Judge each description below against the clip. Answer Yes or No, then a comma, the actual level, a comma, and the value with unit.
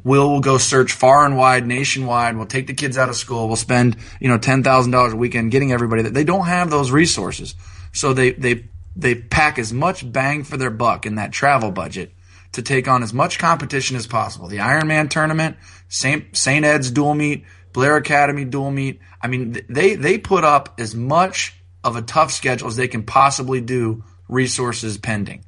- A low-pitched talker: Yes, low, 130 Hz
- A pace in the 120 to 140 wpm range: No, average, 200 wpm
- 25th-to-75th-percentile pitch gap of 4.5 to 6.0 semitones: No, average, 3.6 semitones